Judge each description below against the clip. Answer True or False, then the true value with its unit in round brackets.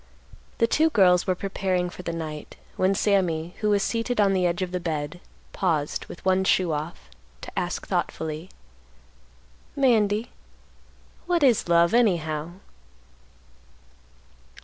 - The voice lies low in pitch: False (185 Hz)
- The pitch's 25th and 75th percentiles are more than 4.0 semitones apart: False (3.7 semitones)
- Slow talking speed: True (130 wpm)